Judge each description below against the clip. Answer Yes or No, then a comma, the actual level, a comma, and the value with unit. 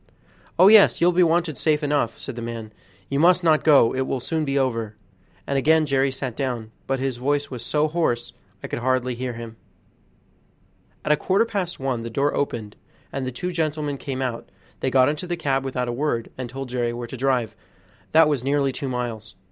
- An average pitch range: Yes, average, 3.8 semitones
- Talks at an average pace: No, fast, 210 wpm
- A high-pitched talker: No, low, 135 Hz